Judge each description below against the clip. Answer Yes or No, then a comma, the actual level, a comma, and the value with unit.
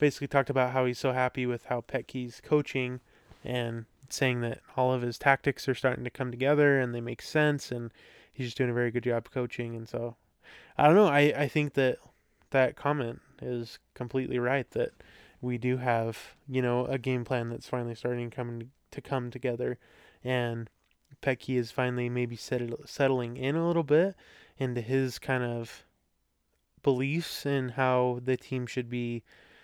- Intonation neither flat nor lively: No, narrow, 2.0 semitones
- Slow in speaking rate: No, average, 175 wpm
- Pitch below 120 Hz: No, low, 125 Hz